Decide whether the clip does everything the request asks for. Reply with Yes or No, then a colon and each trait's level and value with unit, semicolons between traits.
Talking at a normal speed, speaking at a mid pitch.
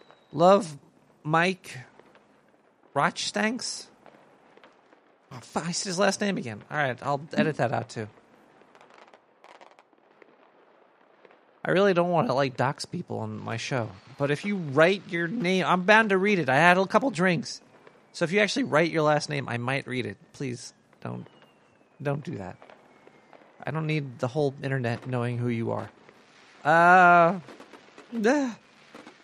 Yes: average, 150 wpm; medium, 155 Hz